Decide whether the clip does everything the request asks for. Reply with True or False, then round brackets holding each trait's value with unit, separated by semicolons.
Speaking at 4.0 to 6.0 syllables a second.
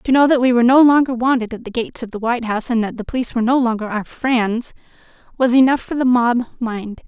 False (6.6 syllables/s)